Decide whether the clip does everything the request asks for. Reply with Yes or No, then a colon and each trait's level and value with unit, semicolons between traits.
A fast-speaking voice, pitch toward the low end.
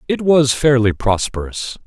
No: slow, 130 wpm; low, 125 Hz